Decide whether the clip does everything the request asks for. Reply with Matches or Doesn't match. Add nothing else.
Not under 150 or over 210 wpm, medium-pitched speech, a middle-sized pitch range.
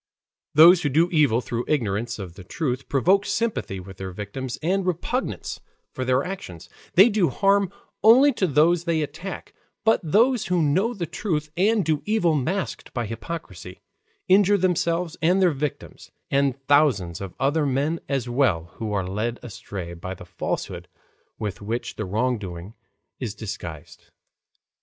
Doesn't match